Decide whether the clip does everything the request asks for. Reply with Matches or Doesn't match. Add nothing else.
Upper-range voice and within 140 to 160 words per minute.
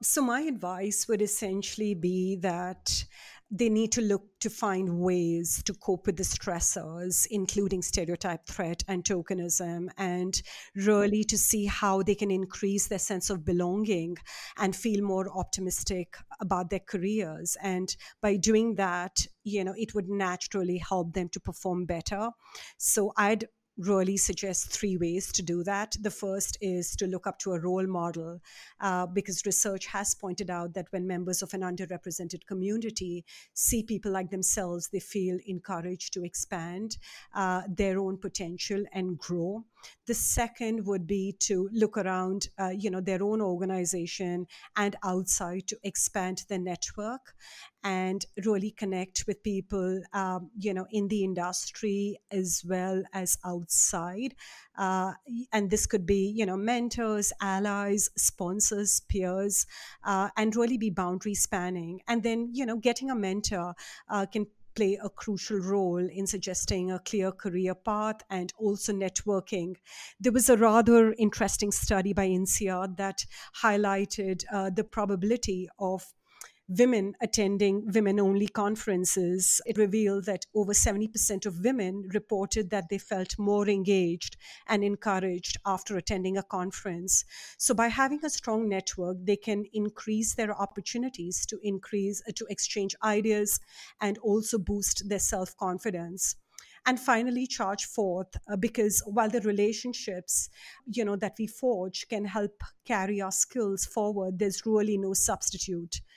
Matches